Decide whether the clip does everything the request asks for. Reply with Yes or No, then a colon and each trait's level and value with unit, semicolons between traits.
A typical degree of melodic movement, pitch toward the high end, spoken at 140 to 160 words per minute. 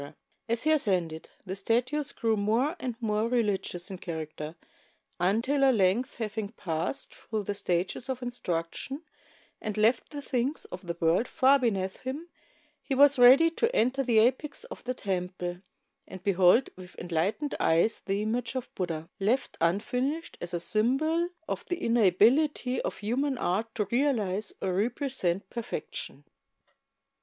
No: wide, 5.9 semitones; high, 220 Hz; average, 150 wpm